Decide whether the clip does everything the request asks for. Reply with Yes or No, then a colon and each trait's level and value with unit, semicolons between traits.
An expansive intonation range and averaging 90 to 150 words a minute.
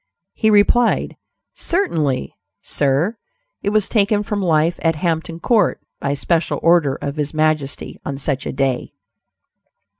Yes: wide, 6.1 semitones; average, 140 wpm